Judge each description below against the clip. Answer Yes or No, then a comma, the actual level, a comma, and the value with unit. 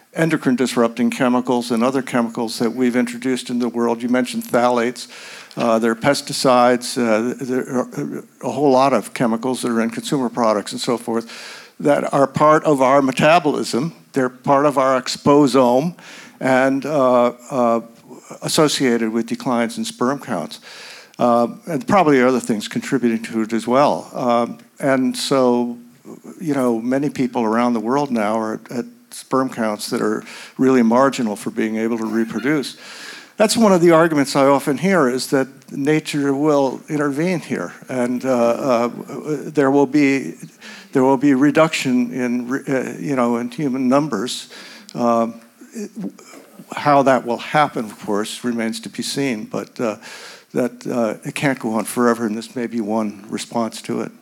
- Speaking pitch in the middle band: No, low, 125 Hz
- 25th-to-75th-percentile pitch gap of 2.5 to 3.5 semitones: Yes, average, 2.9 semitones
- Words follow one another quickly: No, average, 165 wpm